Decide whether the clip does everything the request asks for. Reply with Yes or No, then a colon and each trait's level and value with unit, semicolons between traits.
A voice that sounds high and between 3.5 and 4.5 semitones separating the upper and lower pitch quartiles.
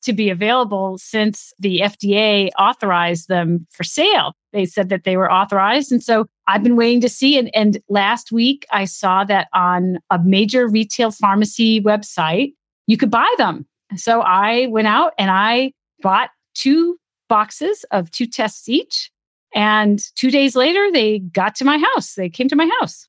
Yes: high, 215 Hz; average, 4.1 semitones